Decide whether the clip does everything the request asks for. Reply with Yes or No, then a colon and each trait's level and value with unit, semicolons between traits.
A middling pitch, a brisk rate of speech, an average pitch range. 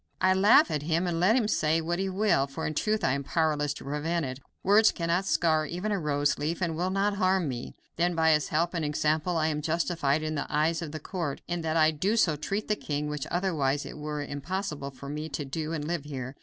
Yes: medium, 160 Hz; fast, 240 wpm; average, 3.2 semitones